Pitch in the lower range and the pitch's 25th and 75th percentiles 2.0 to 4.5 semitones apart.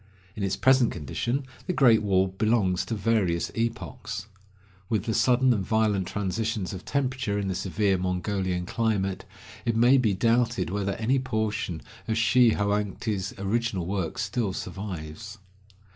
Yes: low, 105 Hz; average, 3.4 semitones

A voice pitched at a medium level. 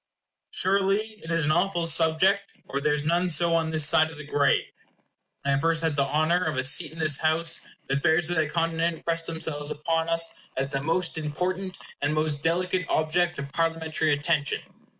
Yes: medium, 160 Hz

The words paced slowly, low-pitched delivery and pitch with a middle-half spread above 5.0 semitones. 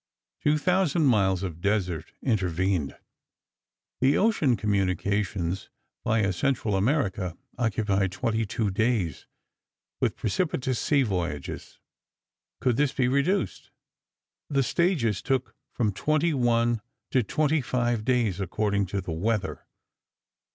Yes: slow, 110 wpm; low, 110 Hz; wide, 5.5 semitones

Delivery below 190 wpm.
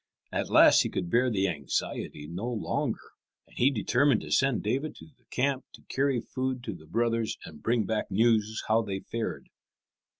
Yes: average, 180 wpm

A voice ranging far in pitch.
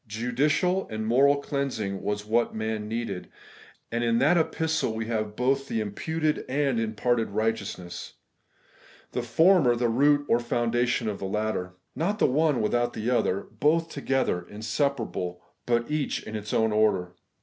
No: average, 4.4 semitones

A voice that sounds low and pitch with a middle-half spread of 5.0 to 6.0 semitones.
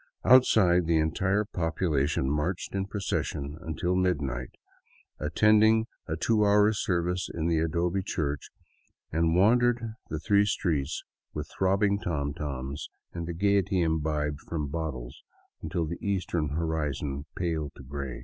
No: very low, 85 Hz; average, 4.5 semitones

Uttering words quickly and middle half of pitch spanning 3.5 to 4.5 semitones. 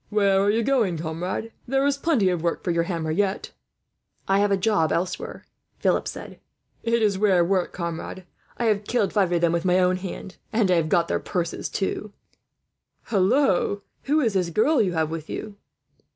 Yes: fast, 210 wpm; average, 3.8 semitones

